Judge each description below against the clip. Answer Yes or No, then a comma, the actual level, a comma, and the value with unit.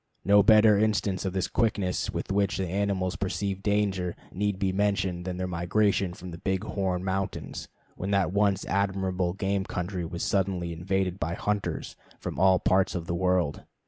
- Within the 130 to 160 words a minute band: No, average, 170 wpm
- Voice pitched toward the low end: Yes, very low, 95 Hz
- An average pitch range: No, narrow, 1.7 semitones